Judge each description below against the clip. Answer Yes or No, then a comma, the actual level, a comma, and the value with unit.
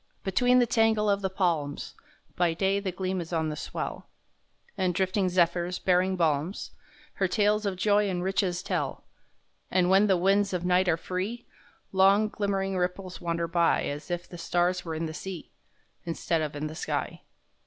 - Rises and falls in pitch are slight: Yes, narrow, 2.3 semitones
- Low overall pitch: No, medium, 185 Hz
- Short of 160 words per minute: No, average, 175 wpm